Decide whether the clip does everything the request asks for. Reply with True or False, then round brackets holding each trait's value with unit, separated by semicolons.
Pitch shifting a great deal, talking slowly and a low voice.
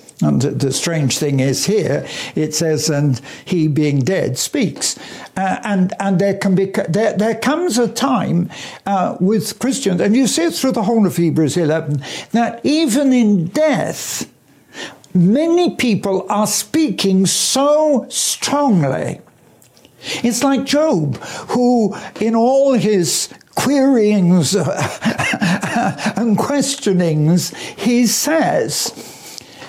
False (6.6 semitones; 120 wpm; 210 Hz)